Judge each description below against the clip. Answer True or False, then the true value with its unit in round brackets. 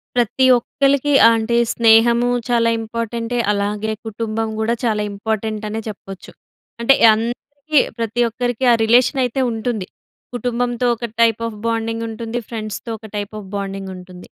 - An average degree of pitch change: False (2.0 semitones)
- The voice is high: True (230 Hz)